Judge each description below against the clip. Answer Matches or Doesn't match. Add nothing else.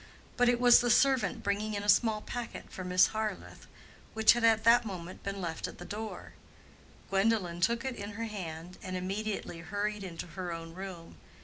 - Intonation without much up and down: Doesn't match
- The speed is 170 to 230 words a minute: Matches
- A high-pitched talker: Matches